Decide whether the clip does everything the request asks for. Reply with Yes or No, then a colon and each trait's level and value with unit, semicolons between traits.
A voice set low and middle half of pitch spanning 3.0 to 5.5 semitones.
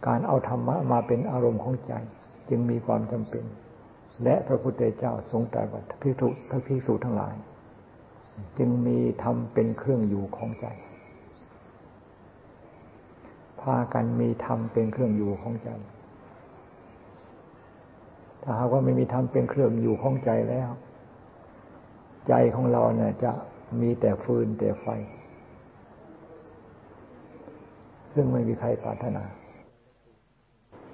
No: low, 115 Hz; narrow, 2.6 semitones